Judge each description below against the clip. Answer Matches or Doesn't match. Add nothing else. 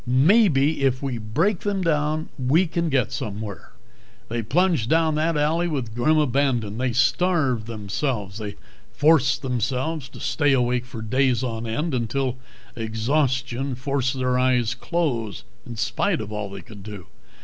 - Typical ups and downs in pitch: Matches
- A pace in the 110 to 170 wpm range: Matches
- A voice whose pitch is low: Matches